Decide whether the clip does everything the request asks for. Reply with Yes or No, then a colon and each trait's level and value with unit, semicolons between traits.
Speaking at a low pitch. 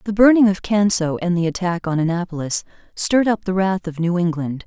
No: medium, 185 Hz